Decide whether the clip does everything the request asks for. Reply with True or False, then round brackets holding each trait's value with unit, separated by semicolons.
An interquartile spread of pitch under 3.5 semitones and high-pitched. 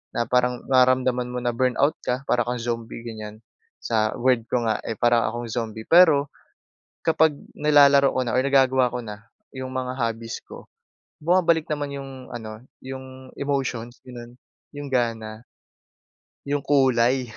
False (2.7 semitones; 125 Hz)